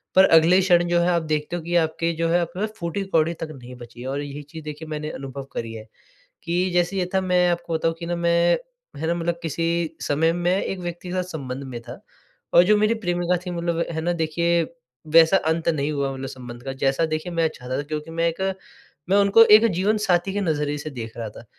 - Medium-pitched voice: Yes, medium, 165 Hz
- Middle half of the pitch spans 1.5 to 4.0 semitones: Yes, average, 2.8 semitones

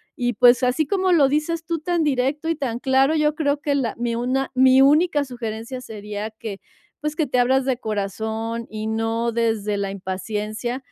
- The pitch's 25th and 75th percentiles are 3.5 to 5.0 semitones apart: Yes, average, 4.4 semitones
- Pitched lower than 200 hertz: No, very high, 250 Hz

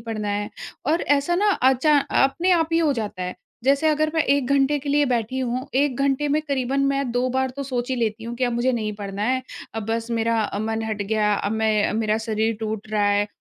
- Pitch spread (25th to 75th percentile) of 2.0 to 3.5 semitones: No, average, 4.2 semitones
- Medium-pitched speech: No, high, 240 Hz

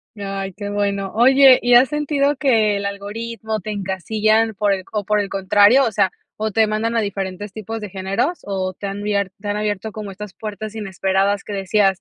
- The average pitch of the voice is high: Yes, high, 205 Hz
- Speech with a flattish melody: Yes, narrow, 2.0 semitones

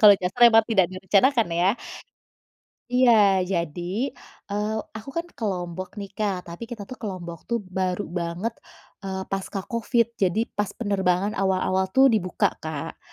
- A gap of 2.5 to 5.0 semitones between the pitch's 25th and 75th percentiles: Yes, average, 3.4 semitones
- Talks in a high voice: Yes, high, 195 Hz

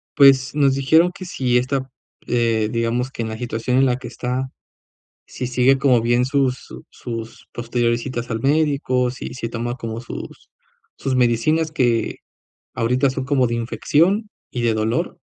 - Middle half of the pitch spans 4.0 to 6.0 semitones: No, narrow, 2.5 semitones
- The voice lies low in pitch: Yes, low, 125 Hz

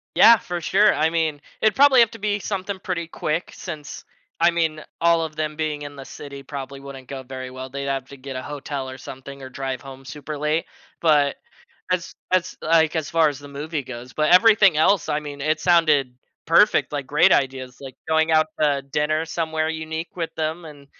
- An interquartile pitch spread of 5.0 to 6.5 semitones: No, average, 3.1 semitones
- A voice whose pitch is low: No, medium, 155 Hz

